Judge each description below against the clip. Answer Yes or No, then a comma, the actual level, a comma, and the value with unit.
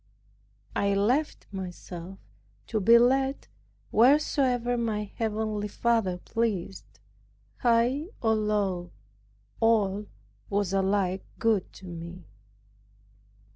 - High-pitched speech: Yes, high, 210 Hz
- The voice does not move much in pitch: No, average, 3.6 semitones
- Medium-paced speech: No, slow, 90 wpm